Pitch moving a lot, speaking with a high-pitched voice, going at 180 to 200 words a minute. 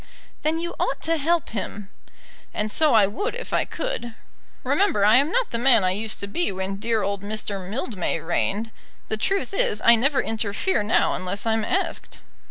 Yes: wide, 6.8 semitones; high, 220 Hz; average, 185 wpm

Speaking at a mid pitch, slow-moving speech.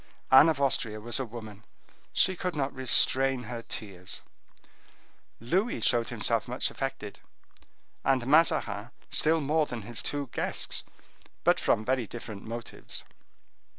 No: low, 125 Hz; slow, 130 wpm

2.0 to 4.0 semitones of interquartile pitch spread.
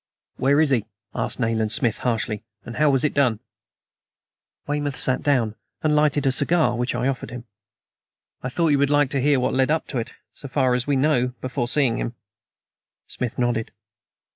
Yes: average, 3.0 semitones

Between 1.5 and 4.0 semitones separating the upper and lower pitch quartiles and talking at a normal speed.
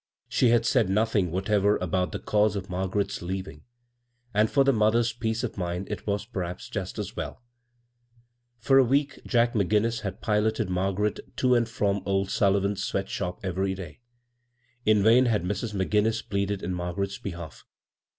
Yes: average, 2.9 semitones; average, 170 wpm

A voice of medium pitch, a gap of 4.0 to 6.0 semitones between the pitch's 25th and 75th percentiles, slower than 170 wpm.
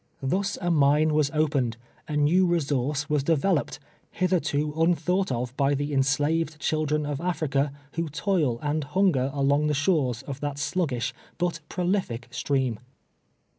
No: medium, 150 Hz; average, 3.0 semitones; average, 150 wpm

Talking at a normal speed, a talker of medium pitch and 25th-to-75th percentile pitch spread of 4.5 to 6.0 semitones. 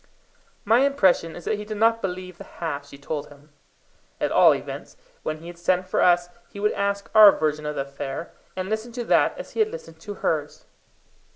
No: fast, 210 wpm; medium, 180 Hz; wide, 5.4 semitones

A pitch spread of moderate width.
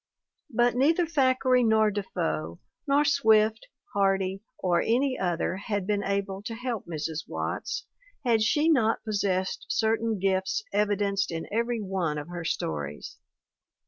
Yes: average, 3.9 semitones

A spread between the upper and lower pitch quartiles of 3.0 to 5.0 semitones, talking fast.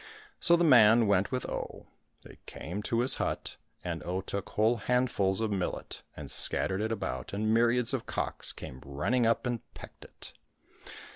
No: average, 3.9 semitones; average, 170 wpm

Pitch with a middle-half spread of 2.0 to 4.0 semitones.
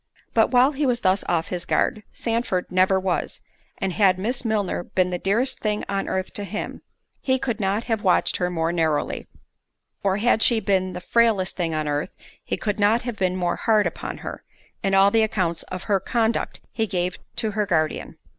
Yes: average, 3.5 semitones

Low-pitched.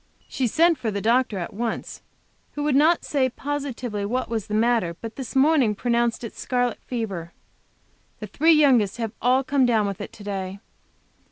No: high, 235 Hz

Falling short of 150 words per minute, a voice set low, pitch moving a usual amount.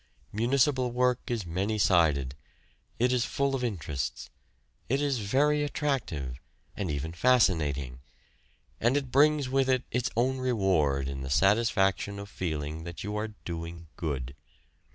No: average, 140 wpm; low, 105 Hz; wide, 8.0 semitones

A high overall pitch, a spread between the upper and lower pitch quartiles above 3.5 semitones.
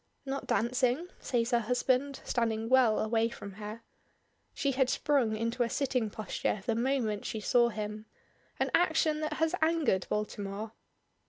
Yes: high, 235 Hz; average, 3.9 semitones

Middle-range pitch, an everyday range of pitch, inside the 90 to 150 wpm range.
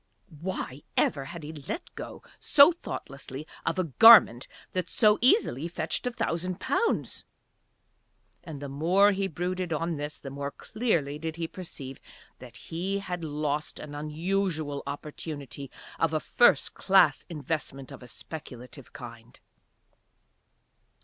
Yes: medium, 155 Hz; average, 4.6 semitones; slow, 135 wpm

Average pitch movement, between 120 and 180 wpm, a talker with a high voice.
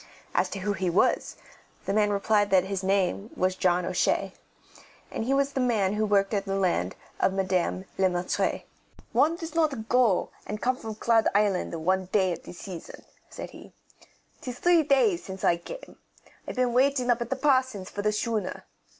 No: average, 4.9 semitones; average, 195 wpm; high, 205 Hz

